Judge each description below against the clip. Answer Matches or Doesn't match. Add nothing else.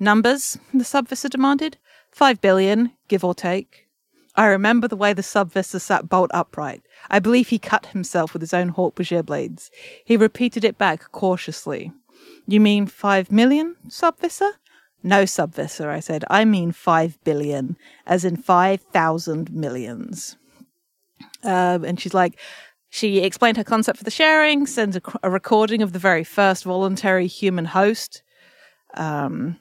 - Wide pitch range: Doesn't match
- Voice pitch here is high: Matches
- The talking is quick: Doesn't match